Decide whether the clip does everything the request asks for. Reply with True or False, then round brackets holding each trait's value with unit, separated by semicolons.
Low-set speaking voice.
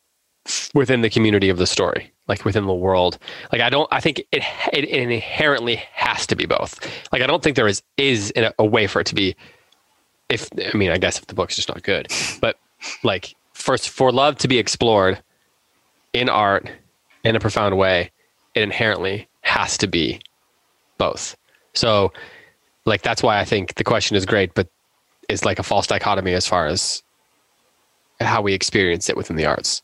True (105 Hz)